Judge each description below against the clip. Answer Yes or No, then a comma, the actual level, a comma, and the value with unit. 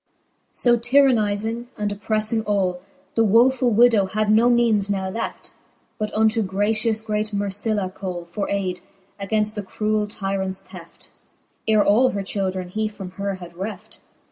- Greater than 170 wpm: No, average, 145 wpm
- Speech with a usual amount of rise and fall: No, narrow, 2.2 semitones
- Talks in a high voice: Yes, high, 210 Hz